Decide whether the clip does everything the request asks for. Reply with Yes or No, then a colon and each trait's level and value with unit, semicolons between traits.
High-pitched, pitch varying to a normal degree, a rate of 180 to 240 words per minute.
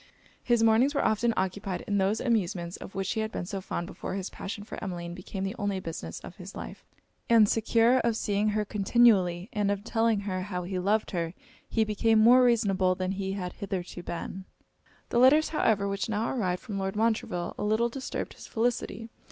Yes: high, 205 Hz; average, 3.2 semitones; average, 195 wpm